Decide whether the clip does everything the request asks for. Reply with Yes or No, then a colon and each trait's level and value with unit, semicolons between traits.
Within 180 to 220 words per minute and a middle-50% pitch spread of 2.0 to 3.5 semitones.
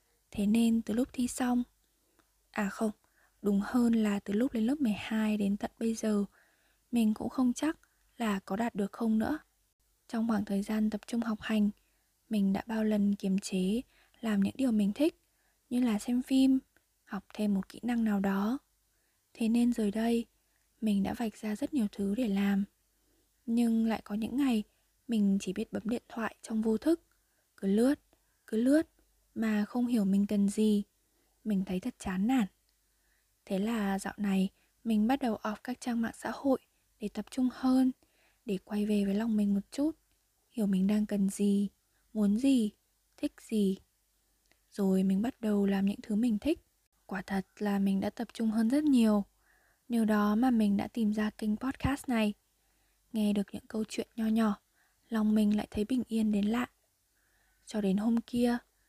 Yes: average, 185 wpm; average, 2.9 semitones